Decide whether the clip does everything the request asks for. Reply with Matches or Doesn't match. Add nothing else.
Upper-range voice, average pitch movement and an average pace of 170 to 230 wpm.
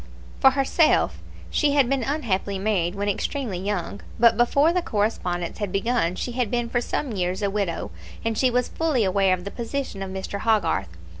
Matches